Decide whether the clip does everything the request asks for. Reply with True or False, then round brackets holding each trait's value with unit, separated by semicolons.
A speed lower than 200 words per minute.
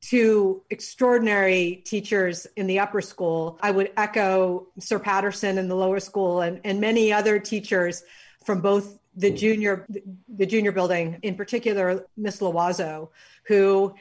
True (140 wpm)